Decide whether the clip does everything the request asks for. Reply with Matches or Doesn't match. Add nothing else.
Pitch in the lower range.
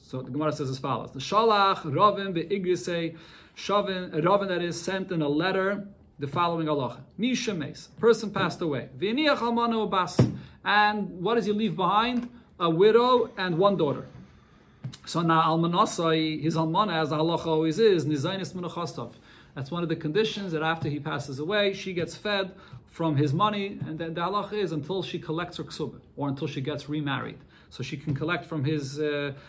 Doesn't match